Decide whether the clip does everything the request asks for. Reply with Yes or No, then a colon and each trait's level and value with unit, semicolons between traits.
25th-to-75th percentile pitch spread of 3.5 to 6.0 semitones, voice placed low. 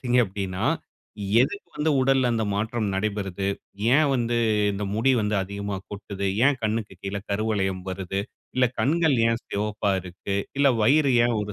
Yes: average, 4.1 semitones; low, 105 Hz